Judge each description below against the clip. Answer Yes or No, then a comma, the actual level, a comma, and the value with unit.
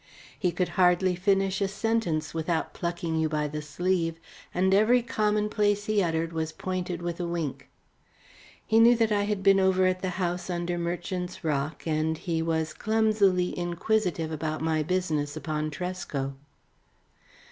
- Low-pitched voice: No, medium, 180 Hz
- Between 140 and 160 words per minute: Yes, average, 155 wpm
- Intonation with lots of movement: No, average, 3.2 semitones